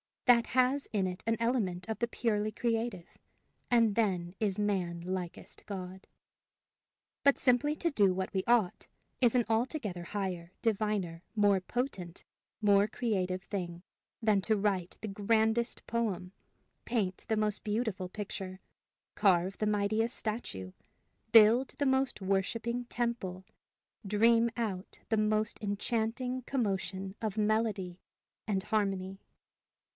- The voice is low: No, high, 210 Hz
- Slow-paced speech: Yes, slow, 125 wpm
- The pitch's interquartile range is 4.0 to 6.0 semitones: No, average, 3.6 semitones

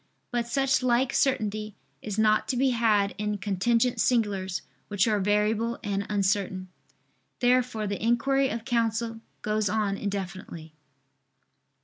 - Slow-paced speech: Yes, slow, 125 wpm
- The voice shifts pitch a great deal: No, average, 2.9 semitones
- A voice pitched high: Yes, high, 215 Hz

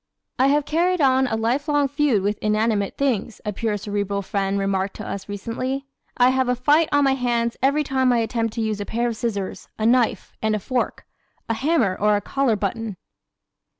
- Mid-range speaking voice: No, high, 230 Hz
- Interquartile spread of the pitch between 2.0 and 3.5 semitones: No, average, 4.3 semitones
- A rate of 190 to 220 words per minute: Yes, average, 200 wpm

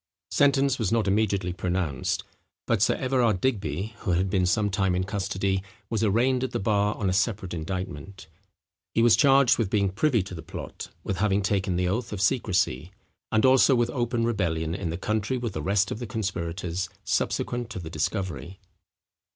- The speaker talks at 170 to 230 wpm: Yes, average, 175 wpm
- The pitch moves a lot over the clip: No, average, 3.9 semitones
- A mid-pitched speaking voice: No, low, 100 Hz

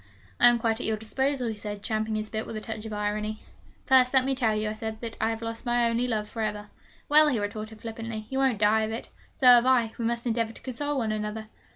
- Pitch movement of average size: No, narrow, 2.0 semitones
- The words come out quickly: Yes, fast, 260 wpm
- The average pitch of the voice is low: No, high, 225 Hz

